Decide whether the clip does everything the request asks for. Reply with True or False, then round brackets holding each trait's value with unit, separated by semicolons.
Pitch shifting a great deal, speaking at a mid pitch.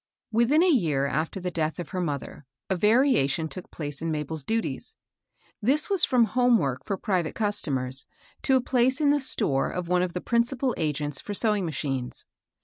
True (8.0 semitones; 180 Hz)